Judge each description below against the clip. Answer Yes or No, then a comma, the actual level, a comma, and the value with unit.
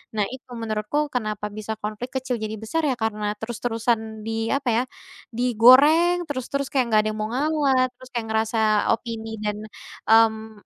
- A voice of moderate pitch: No, high, 230 Hz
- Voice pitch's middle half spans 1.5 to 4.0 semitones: Yes, average, 3.0 semitones